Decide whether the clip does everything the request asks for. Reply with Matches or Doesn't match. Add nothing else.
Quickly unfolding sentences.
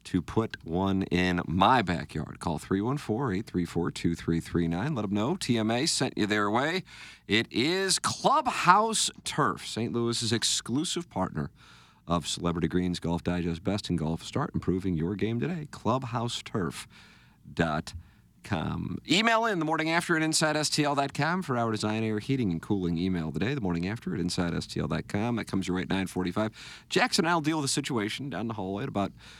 Doesn't match